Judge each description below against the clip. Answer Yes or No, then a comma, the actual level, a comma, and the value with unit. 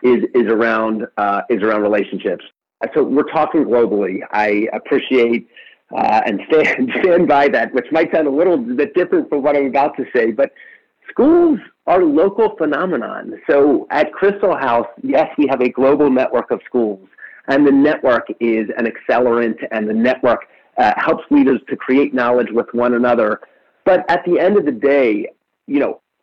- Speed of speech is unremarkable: Yes, average, 175 wpm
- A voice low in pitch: Yes, low, 125 Hz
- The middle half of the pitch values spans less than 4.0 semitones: No, average, 4.3 semitones